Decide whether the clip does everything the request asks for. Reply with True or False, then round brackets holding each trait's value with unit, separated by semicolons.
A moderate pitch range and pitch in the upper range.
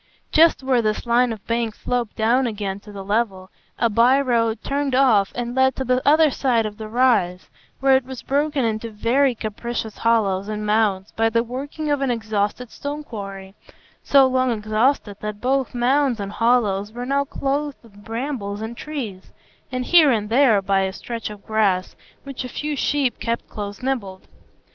True (3.9 semitones; 235 Hz)